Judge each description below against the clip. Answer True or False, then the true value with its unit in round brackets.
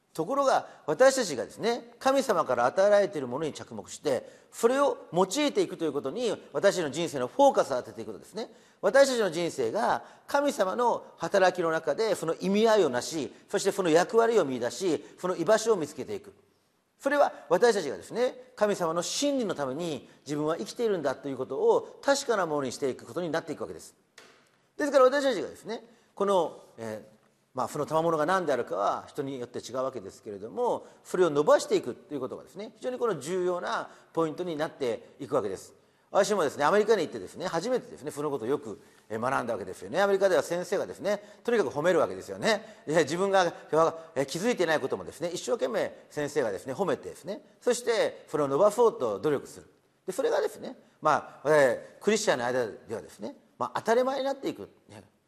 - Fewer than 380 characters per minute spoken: False (430 characters per minute)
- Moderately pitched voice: False (200 Hz)